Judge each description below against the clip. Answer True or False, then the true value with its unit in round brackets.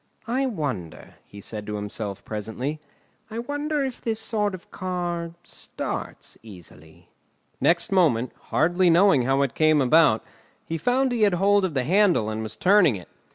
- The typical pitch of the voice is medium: True (165 Hz)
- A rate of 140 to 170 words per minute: True (160 wpm)